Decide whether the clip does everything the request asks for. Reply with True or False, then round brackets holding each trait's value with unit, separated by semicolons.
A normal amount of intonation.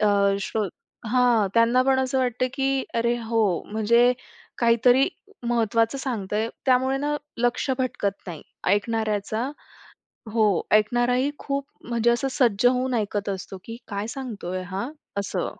True (3.1 semitones)